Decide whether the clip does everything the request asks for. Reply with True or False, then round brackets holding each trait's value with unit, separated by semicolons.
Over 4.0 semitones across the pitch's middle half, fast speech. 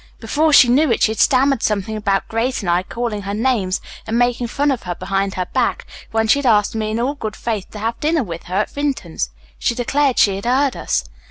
True (4.4 semitones; 240 wpm)